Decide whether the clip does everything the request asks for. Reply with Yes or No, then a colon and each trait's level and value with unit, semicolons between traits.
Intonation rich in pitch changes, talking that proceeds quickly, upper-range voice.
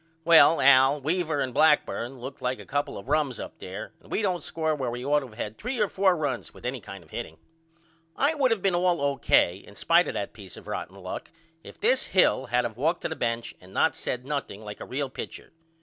No: wide, 5.7 semitones; fast, 240 wpm; medium, 140 Hz